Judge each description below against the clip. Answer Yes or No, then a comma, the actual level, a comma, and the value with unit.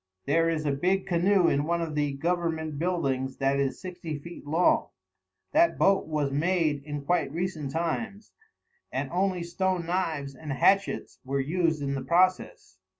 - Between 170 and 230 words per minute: No, average, 160 wpm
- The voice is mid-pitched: Yes, medium, 165 Hz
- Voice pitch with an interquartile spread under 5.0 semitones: Yes, average, 4.0 semitones